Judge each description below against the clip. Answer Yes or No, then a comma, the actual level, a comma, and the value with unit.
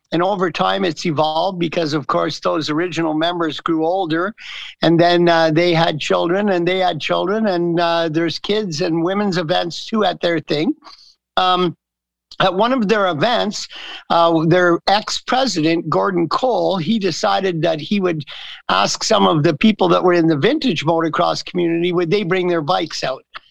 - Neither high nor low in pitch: Yes, medium, 175 Hz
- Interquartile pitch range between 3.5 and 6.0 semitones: No, narrow, 2.5 semitones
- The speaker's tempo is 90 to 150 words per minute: No, average, 175 wpm